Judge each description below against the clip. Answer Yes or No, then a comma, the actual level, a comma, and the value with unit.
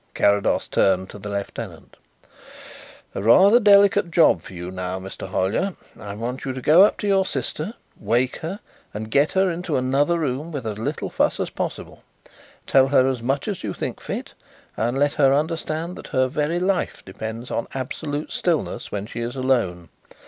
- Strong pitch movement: Yes, wide, 7.2 semitones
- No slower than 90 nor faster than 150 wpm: No, average, 180 wpm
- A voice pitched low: Yes, low, 130 Hz